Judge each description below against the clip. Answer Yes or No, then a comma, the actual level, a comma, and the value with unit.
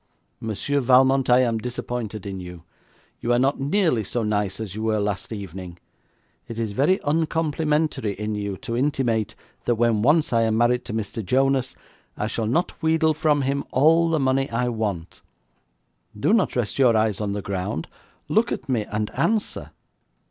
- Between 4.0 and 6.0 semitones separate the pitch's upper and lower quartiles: Yes, average, 4.7 semitones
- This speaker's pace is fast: No, average, 175 wpm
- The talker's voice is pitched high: No, low, 120 Hz